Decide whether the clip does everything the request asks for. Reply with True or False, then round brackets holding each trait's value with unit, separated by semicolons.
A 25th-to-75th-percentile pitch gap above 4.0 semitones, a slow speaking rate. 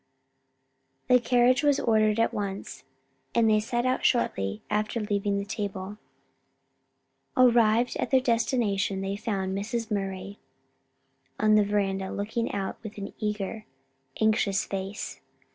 False (2.7 semitones; 125 wpm)